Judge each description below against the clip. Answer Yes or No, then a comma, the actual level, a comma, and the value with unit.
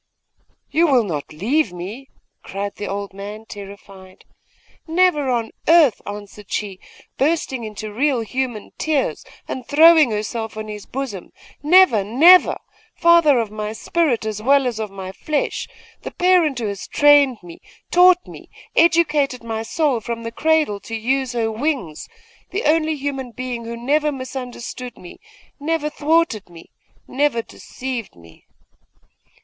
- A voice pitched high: Yes, high, 245 Hz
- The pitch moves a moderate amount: No, wide, 6.0 semitones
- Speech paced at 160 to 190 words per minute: No, average, 145 wpm